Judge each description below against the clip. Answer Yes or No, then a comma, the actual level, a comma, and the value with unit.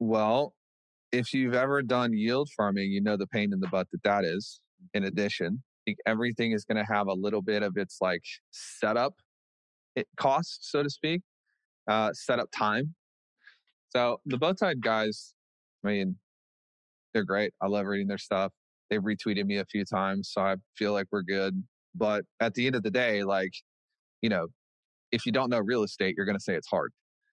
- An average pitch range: Yes, average, 3.3 semitones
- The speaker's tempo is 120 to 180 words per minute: No, average, 195 wpm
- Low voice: Yes, low, 105 Hz